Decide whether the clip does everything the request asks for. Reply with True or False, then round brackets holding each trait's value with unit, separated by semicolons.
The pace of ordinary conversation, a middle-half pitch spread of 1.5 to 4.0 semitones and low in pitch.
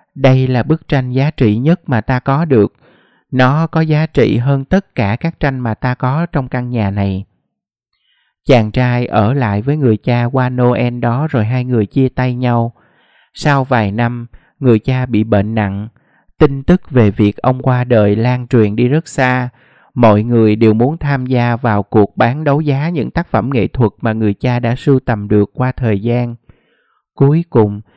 True (195 wpm; 3.5 semitones; 125 Hz)